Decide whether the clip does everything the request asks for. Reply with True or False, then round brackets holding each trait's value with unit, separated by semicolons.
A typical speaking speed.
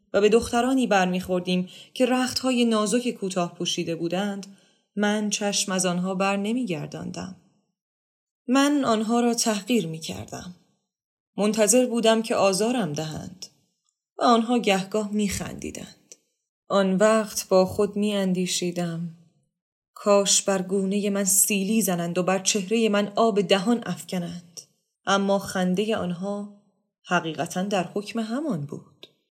True (115 wpm)